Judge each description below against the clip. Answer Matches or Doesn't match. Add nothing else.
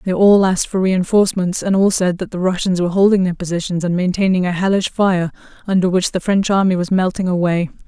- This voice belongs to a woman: Matches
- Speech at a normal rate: Doesn't match